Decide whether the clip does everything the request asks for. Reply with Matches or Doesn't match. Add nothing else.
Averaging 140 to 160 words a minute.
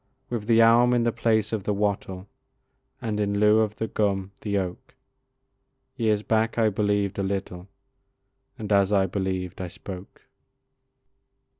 Matches